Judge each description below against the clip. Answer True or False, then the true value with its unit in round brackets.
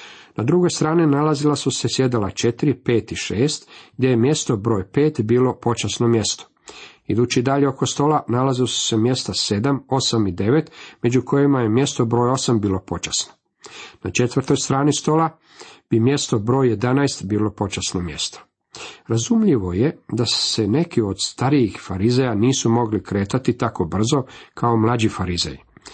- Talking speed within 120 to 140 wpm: False (155 wpm)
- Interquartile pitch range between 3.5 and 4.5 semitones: True (4.1 semitones)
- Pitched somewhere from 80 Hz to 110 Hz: False (120 Hz)